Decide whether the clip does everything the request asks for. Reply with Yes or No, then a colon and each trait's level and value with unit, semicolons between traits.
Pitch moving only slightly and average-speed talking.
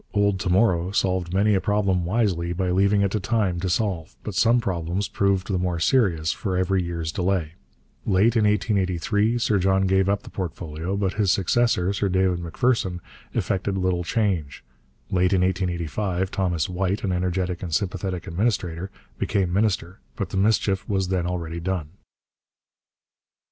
Yes: narrow, 2.2 semitones; average, 160 wpm